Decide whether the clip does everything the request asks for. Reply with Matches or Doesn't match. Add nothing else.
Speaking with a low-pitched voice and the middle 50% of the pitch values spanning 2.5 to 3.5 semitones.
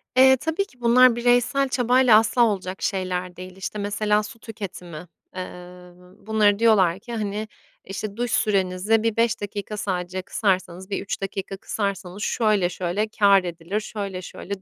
Doesn't match